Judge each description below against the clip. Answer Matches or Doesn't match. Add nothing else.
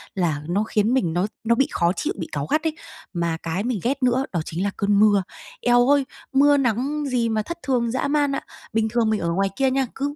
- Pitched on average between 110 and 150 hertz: Doesn't match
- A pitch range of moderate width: Doesn't match